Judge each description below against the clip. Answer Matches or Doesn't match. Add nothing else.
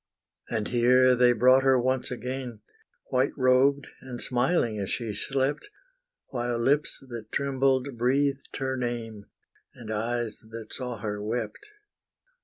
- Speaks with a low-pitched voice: Matches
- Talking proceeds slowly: Matches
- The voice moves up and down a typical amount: Doesn't match